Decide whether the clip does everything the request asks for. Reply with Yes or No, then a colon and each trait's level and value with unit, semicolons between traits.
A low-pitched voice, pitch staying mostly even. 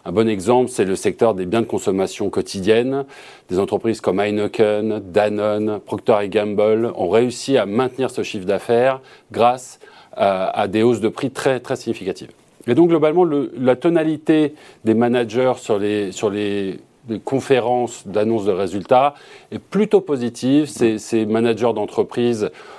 No: low, 115 Hz; average, 3.6 semitones